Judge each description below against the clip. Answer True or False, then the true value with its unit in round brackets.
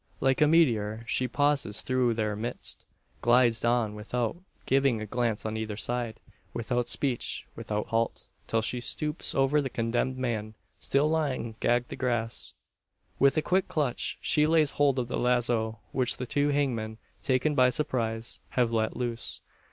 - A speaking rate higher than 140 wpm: True (160 wpm)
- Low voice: True (120 Hz)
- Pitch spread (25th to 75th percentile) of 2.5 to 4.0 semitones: True (3.1 semitones)